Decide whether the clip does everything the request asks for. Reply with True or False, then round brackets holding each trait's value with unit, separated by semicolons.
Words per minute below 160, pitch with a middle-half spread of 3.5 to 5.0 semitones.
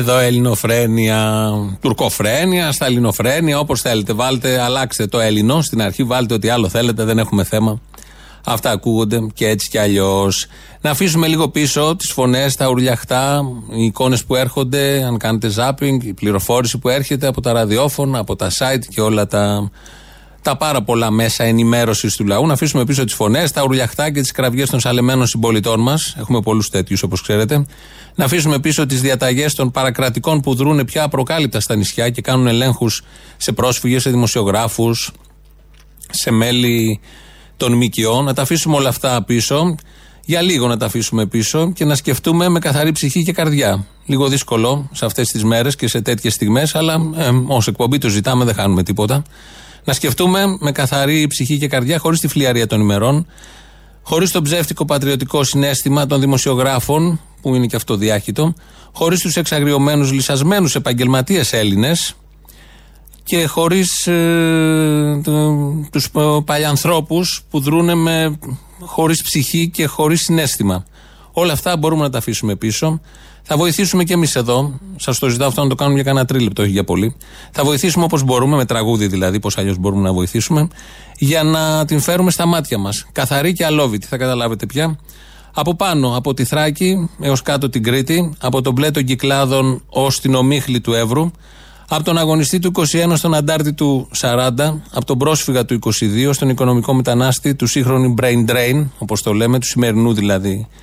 False (170 wpm; 4.7 semitones)